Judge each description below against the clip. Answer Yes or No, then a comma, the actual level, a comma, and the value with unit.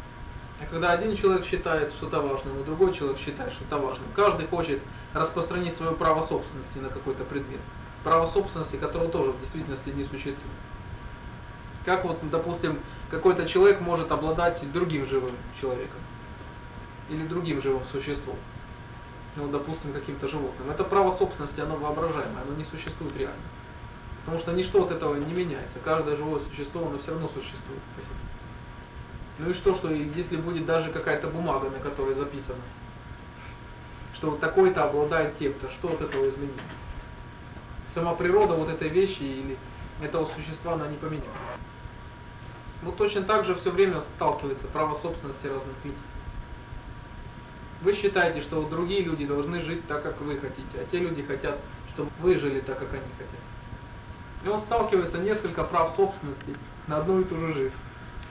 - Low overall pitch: No, medium, 150 Hz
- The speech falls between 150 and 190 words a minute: Yes, average, 155 wpm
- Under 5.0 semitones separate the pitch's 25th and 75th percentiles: Yes, average, 3.9 semitones